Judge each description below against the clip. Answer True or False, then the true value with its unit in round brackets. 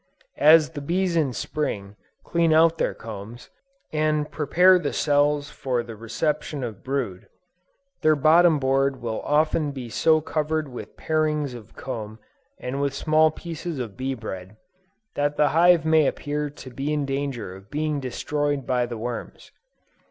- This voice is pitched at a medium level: True (145 Hz)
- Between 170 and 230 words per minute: False (155 wpm)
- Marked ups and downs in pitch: False (4.0 semitones)